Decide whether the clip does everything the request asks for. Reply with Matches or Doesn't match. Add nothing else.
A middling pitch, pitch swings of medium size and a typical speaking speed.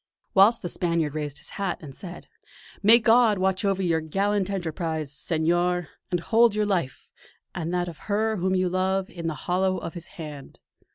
Matches